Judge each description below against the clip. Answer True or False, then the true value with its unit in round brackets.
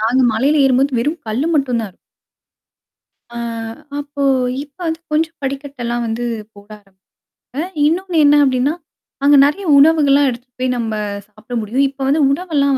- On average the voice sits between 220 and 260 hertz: False (275 Hz)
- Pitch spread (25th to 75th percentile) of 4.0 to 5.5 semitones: False (3.4 semitones)